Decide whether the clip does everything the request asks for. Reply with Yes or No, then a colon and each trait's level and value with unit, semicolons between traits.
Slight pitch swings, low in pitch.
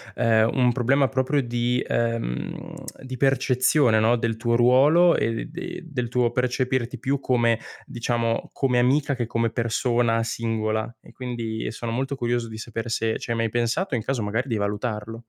Yes: narrow, 2.1 semitones; low, 120 Hz